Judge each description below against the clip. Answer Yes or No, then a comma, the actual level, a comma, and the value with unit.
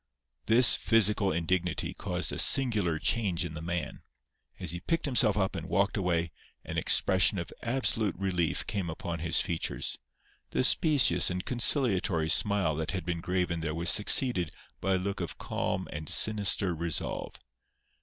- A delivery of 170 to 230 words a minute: No, average, 155 wpm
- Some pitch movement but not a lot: Yes, average, 3.9 semitones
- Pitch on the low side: Yes, very low, 95 Hz